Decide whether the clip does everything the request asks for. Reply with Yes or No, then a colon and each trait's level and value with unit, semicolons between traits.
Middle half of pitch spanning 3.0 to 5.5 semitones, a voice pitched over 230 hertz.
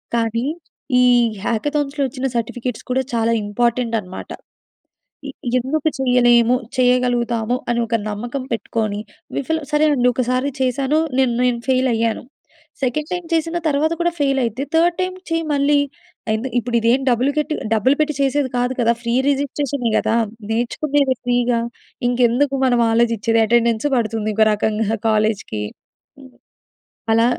Yes: average, 3.3 semitones; high, 245 Hz